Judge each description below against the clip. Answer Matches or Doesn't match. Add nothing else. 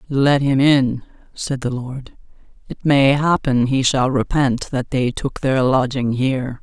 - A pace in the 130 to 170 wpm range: Matches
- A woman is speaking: Matches